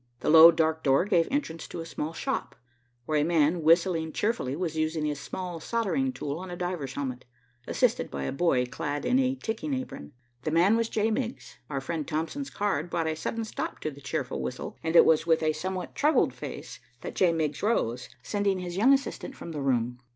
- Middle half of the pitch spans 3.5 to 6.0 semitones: Yes, average, 5.1 semitones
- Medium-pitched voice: Yes, medium, 165 Hz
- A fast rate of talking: Yes, fast, 210 wpm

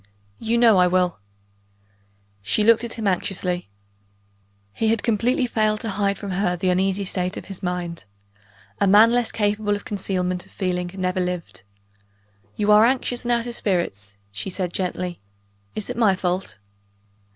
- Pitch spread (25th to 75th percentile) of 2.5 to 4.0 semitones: Yes, average, 3.2 semitones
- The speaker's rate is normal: Yes, average, 165 wpm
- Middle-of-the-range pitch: No, high, 195 Hz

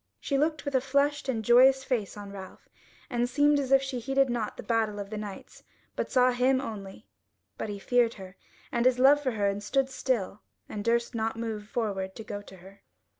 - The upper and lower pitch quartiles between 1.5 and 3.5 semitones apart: No, average, 4.4 semitones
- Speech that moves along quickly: Yes, fast, 215 wpm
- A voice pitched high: Yes, high, 235 Hz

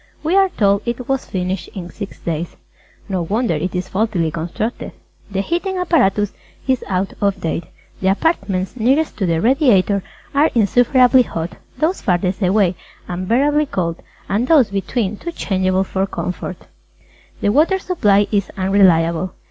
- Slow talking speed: No, average, 150 wpm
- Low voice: No, high, 200 Hz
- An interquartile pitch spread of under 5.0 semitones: No, wide, 5.5 semitones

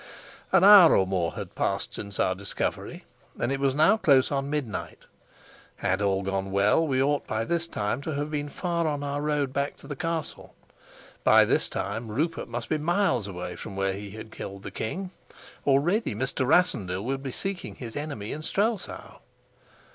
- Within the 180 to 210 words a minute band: Yes, average, 185 wpm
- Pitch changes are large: Yes, wide, 7.2 semitones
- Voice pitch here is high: No, low, 135 Hz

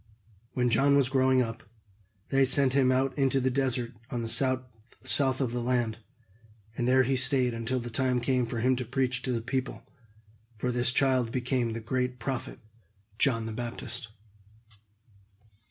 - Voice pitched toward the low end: Yes, low, 125 Hz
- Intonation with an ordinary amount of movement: No, narrow, 1.7 semitones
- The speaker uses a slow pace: No, average, 165 wpm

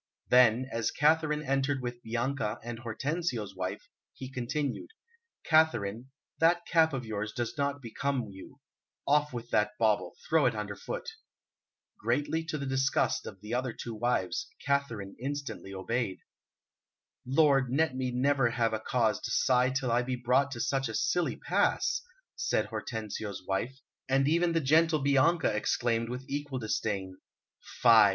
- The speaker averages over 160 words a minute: No, average, 150 wpm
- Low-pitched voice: Yes, low, 125 Hz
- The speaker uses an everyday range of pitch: Yes, average, 3.9 semitones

